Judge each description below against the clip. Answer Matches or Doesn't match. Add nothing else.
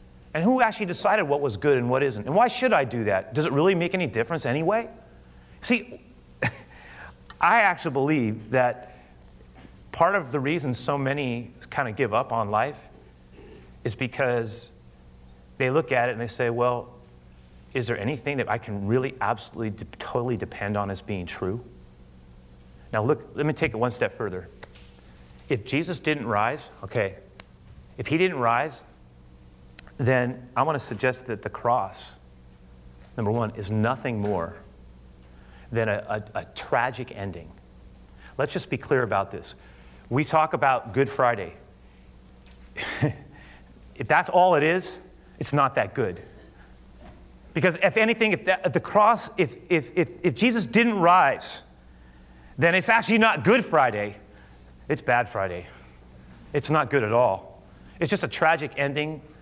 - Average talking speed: Matches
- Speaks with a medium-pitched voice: Doesn't match